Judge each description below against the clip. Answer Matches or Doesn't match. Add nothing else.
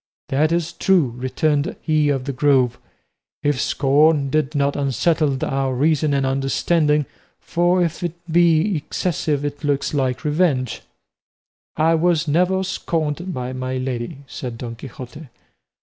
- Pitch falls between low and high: Matches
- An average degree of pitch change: Matches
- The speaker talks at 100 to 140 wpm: Matches